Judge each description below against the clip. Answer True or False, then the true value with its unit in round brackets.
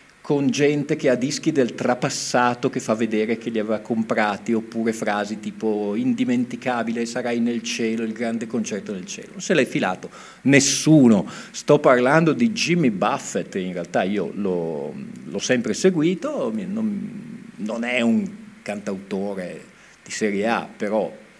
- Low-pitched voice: True (130 Hz)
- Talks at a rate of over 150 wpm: False (145 wpm)